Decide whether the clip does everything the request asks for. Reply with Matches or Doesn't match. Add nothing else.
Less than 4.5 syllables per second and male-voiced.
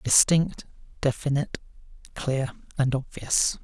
Matches